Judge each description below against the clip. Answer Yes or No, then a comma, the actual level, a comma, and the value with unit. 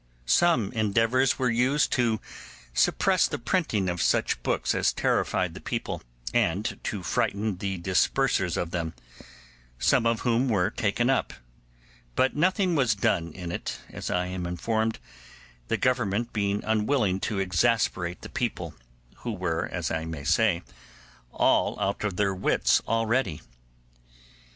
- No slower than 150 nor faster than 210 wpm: No, average, 140 wpm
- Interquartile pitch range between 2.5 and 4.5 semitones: No, average, 4.9 semitones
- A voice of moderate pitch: No, low, 105 Hz